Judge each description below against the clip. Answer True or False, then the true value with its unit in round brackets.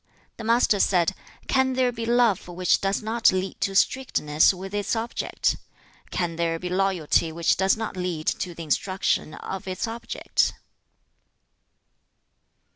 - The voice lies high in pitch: True (195 Hz)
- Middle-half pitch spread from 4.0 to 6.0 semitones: True (4.4 semitones)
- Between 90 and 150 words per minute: True (140 wpm)